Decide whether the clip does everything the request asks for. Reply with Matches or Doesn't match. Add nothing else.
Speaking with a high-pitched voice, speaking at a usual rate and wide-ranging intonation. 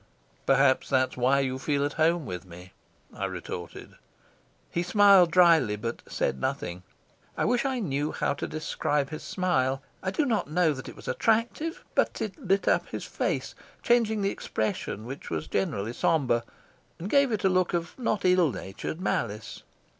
Doesn't match